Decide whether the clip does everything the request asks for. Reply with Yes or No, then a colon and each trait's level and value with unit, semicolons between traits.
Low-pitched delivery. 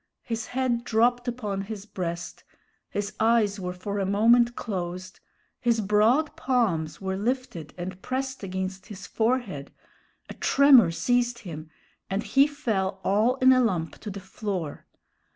No: high, 210 Hz